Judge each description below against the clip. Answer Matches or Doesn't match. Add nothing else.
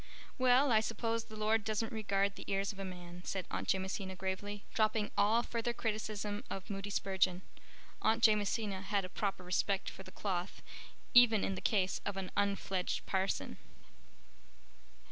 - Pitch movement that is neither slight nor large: Doesn't match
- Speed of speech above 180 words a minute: Doesn't match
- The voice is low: Doesn't match